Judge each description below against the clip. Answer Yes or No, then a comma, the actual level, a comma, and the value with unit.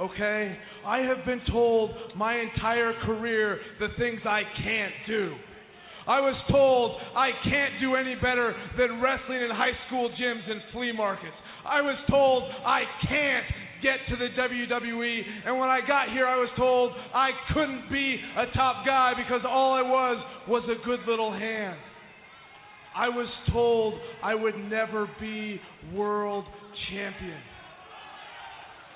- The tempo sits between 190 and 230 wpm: No, average, 145 wpm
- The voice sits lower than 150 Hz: No, high, 240 Hz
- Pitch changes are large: No, average, 2.9 semitones